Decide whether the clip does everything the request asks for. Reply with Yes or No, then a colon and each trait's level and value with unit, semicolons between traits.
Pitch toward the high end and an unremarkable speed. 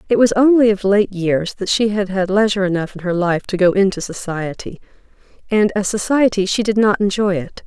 No: high, 200 Hz; fast, 210 wpm